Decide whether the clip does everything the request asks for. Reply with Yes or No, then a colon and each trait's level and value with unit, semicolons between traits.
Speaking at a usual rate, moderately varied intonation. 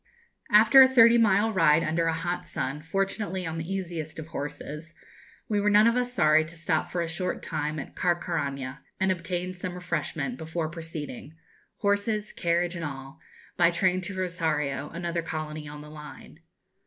Yes: average, 170 wpm; average, 3.4 semitones